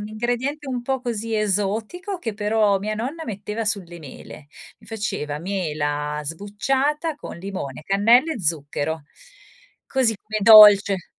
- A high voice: Yes, high, 210 Hz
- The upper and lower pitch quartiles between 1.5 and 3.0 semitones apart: No, average, 4.6 semitones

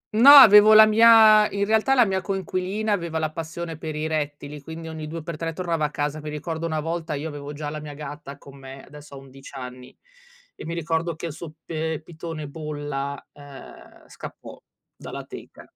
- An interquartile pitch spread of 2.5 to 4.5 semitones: Yes, average, 2.8 semitones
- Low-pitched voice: No, medium, 160 Hz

